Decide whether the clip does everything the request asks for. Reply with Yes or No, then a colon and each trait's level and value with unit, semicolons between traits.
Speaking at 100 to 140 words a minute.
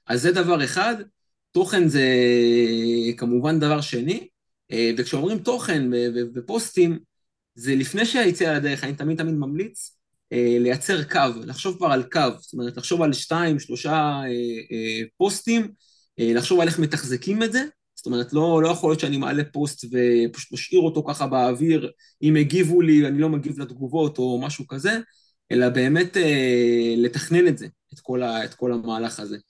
No: fast, 150 wpm